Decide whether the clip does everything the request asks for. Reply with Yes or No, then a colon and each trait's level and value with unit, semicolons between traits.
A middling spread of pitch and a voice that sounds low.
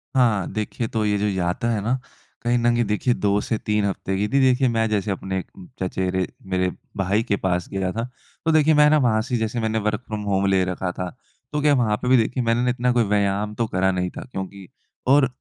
Yes: average, 3.9 semitones; low, 105 Hz